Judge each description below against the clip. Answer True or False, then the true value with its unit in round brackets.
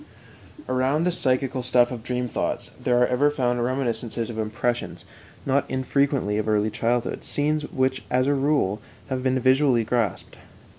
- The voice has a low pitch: True (125 Hz)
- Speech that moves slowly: False (155 wpm)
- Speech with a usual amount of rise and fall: False (2.2 semitones)